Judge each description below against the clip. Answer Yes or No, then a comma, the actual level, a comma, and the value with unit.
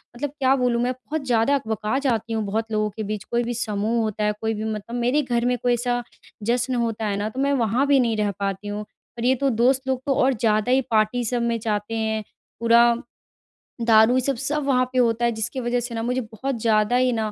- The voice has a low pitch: No, high, 235 Hz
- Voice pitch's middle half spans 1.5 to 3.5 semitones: Yes, average, 2.7 semitones